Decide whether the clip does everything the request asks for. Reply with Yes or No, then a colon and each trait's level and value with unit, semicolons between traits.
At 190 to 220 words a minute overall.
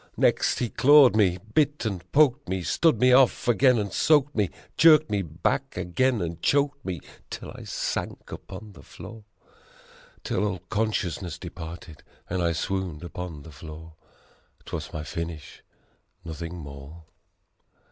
No: average, 145 wpm